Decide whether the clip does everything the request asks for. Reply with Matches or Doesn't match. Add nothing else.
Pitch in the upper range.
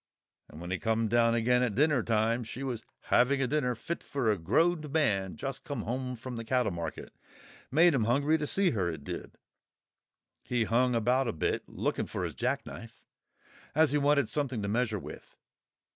Doesn't match